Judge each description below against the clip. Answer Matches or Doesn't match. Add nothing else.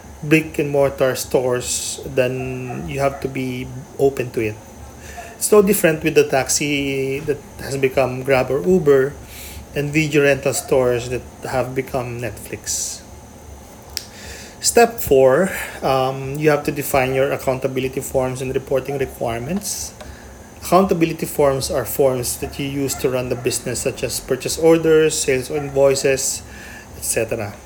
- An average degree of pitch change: Doesn't match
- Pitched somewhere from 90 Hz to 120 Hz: Doesn't match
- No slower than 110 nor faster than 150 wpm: Matches